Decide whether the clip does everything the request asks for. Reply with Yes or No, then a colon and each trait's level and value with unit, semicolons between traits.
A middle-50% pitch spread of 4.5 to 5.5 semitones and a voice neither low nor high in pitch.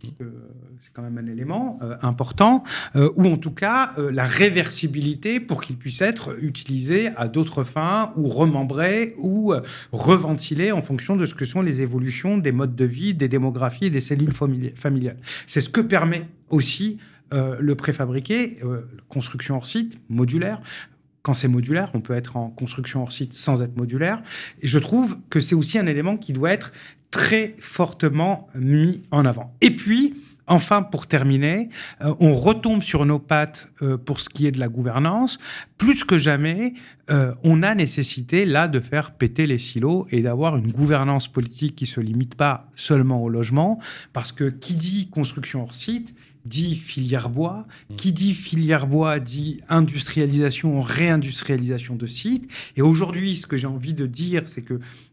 Yes: average, 5.1 semitones; medium, 145 Hz